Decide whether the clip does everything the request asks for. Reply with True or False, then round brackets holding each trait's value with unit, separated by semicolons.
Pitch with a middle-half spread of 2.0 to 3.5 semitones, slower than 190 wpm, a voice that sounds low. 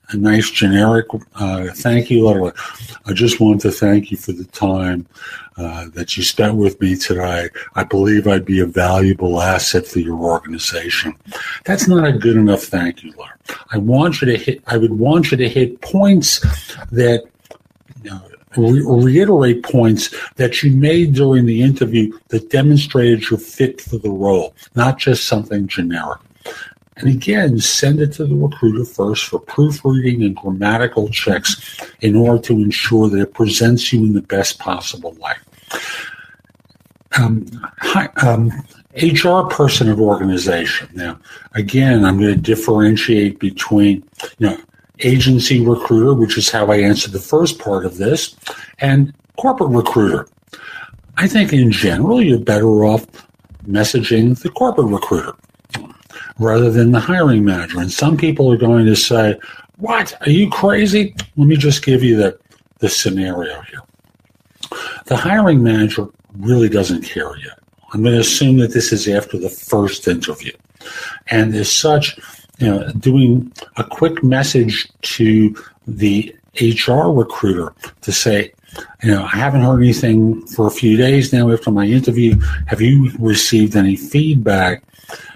False (4.3 semitones; 155 wpm; 115 Hz)